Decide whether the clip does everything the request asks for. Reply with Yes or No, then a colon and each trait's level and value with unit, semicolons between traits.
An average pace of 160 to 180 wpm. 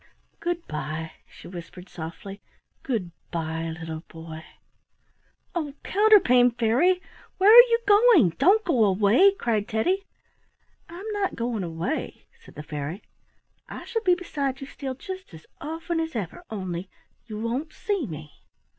No: average, 140 wpm